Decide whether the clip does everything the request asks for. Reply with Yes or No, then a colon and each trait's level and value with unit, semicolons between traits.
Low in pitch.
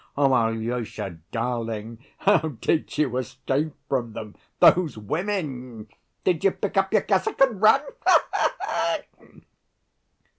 Yes: low, 130 Hz